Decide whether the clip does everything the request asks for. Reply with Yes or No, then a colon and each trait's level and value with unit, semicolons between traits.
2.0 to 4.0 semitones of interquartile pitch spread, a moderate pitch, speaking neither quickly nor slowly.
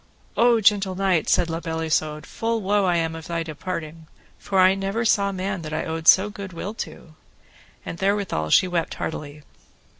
Yes: average, 3.5 semitones; medium, 175 Hz; average, 185 wpm